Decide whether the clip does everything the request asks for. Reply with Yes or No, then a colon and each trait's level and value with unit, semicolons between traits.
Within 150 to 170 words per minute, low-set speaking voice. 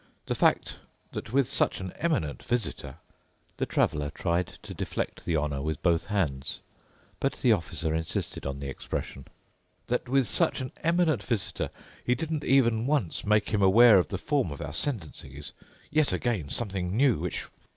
Yes: average, 160 wpm; low, 100 Hz